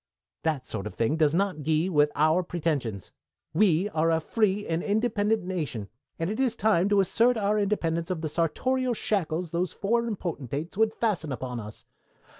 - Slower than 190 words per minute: Yes, average, 175 wpm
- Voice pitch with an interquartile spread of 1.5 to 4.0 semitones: No, average, 5.1 semitones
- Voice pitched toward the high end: No, medium, 170 Hz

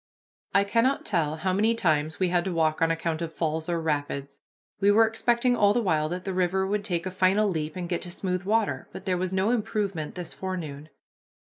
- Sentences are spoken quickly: Yes, fast, 220 wpm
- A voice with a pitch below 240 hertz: Yes, medium, 185 Hz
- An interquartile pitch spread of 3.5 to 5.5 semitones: Yes, average, 3.8 semitones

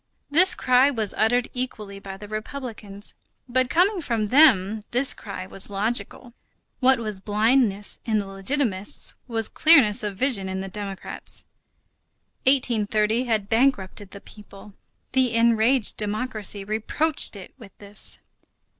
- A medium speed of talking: No, slow, 130 wpm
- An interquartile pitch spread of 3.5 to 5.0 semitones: Yes, average, 3.9 semitones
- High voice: Yes, high, 220 Hz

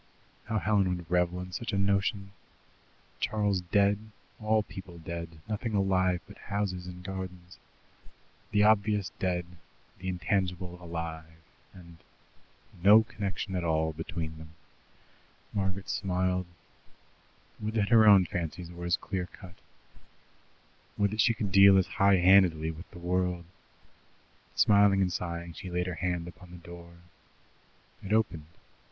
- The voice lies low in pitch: Yes, very low, 90 Hz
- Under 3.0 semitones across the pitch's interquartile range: Yes, narrow, 2.4 semitones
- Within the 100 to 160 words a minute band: Yes, slow, 135 wpm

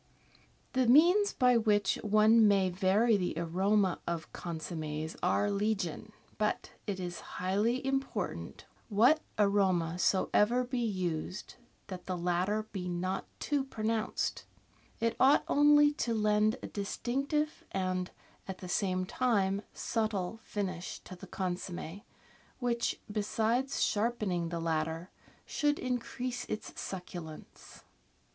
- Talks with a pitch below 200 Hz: No, high, 205 Hz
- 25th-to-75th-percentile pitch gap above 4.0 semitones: Yes, average, 4.5 semitones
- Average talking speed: No, slow, 120 wpm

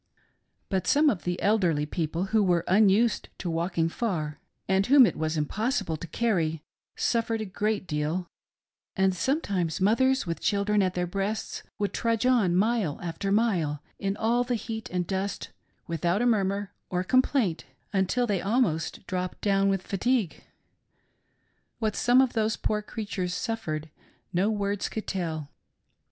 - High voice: Yes, high, 195 Hz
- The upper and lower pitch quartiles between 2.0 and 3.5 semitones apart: No, average, 4.1 semitones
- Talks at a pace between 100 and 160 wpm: Yes, average, 155 wpm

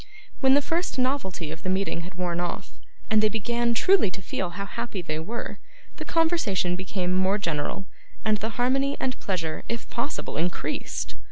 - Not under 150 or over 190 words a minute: Yes, average, 175 wpm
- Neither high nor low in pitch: No, high, 200 Hz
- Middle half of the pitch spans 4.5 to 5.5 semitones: Yes, average, 5.2 semitones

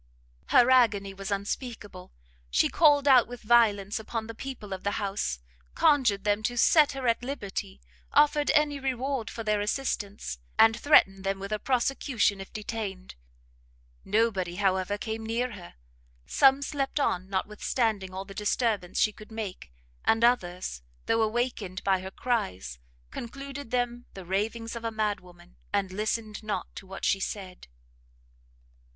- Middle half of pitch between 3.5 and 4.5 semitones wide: Yes, average, 3.9 semitones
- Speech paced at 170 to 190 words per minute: No, average, 150 wpm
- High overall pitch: Yes, high, 215 Hz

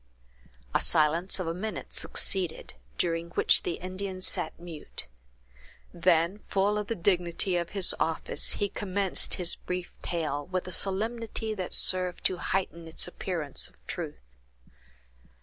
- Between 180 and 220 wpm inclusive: No, average, 140 wpm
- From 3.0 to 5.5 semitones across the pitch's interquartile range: No, narrow, 2.4 semitones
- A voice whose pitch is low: No, medium, 180 Hz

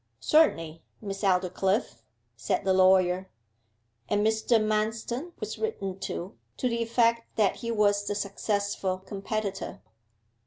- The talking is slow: Yes, slow, 120 wpm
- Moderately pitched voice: No, high, 205 Hz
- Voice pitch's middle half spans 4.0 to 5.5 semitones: No, average, 2.9 semitones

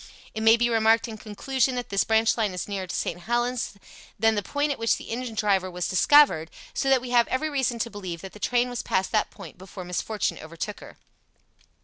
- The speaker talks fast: Yes, fast, 225 wpm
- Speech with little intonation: No, average, 4.1 semitones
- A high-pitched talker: Yes, high, 225 Hz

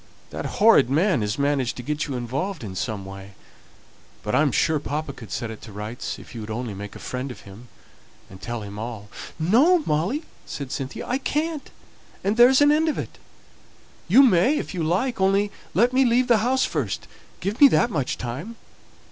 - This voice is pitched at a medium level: Yes, medium, 150 Hz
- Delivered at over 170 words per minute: Yes, fast, 205 wpm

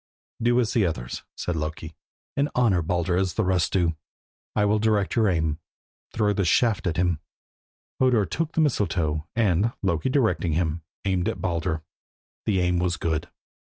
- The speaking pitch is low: Yes, very low, 90 Hz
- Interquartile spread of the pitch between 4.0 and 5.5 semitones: Yes, average, 4.6 semitones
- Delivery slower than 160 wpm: No, average, 165 wpm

